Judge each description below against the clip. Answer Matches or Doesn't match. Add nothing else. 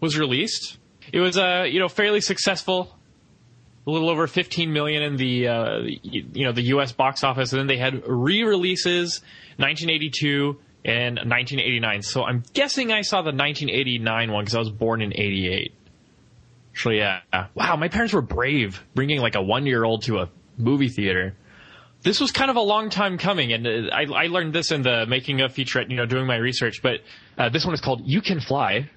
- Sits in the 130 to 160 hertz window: Matches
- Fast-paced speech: Matches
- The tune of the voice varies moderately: Doesn't match